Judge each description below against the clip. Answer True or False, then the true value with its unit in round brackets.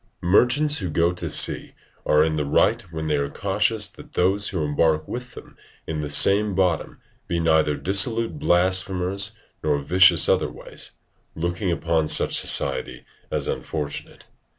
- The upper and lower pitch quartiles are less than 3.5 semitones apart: False (4.1 semitones)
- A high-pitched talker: False (90 Hz)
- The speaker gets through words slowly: False (150 wpm)